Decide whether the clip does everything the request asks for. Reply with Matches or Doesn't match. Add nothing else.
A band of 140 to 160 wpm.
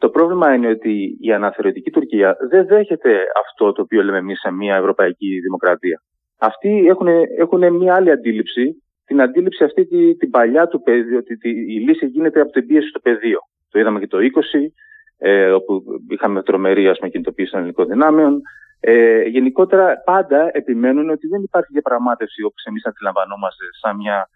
Doesn't match